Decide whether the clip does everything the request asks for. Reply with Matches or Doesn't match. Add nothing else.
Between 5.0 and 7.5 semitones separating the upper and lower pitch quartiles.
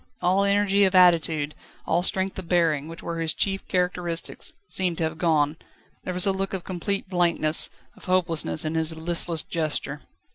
Doesn't match